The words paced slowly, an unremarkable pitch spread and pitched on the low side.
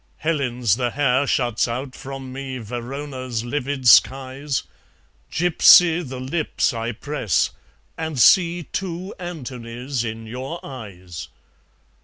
Yes: slow, 110 wpm; average, 3.6 semitones; low, 130 Hz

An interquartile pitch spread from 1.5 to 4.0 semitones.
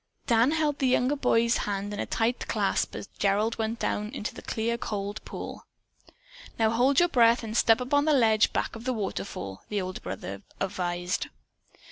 Yes: average, 3.5 semitones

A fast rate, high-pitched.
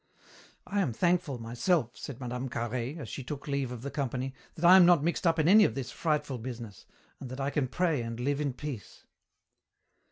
No: fast, 210 wpm; low, 135 Hz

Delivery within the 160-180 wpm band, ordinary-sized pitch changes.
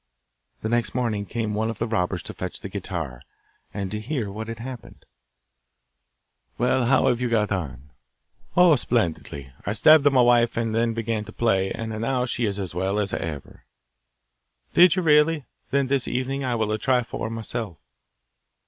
Yes: average, 175 wpm; average, 3.8 semitones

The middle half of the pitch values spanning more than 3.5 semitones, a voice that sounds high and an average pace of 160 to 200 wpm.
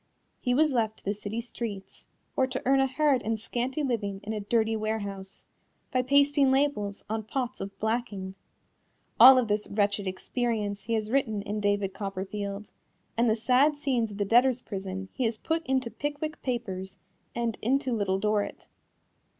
Yes: average, 4.1 semitones; high, 225 Hz; average, 170 wpm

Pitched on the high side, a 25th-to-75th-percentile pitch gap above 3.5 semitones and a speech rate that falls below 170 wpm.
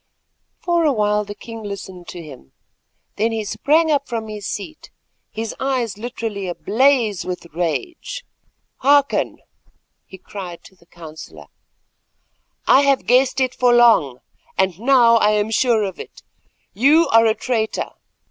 Yes: high, 225 Hz; average, 5.1 semitones; average, 140 wpm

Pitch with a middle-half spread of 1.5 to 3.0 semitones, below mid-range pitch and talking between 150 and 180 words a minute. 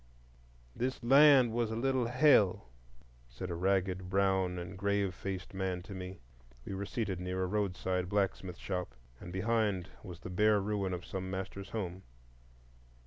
Yes: narrow, 2.6 semitones; very low, 95 Hz; average, 155 wpm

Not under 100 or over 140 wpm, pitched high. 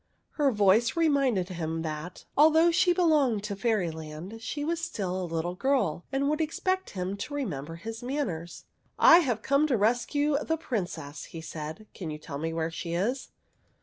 No: average, 185 wpm; high, 215 Hz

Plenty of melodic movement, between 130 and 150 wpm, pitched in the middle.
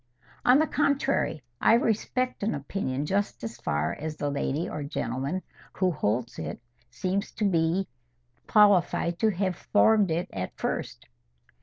Yes: wide, 6.7 semitones; average, 140 wpm; medium, 175 Hz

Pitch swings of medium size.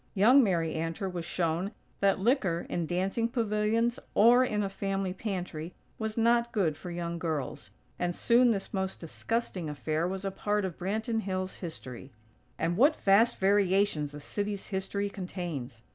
Yes: average, 3.8 semitones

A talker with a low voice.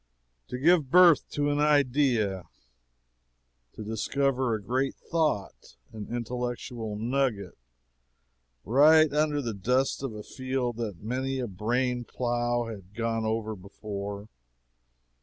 Yes: low, 120 Hz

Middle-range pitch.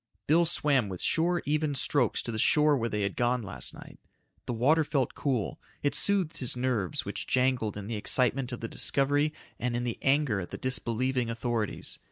No: low, 125 Hz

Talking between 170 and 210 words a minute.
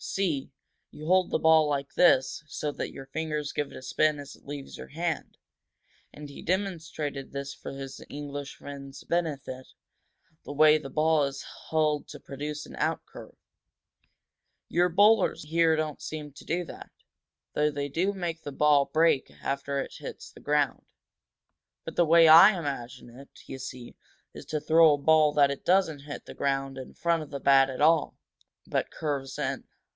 Yes: average, 175 wpm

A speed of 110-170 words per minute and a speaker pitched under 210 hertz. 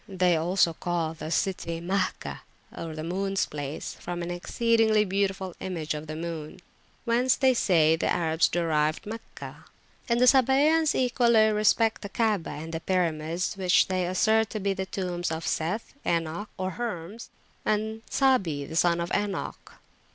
Yes: average, 150 wpm; medium, 185 Hz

